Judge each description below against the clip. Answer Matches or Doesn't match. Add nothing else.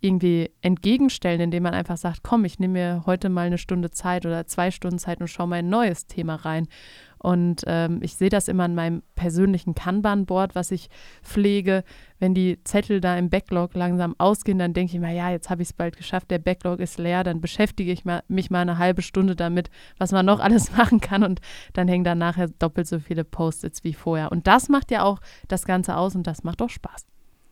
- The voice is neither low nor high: Matches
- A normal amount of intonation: Doesn't match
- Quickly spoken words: Matches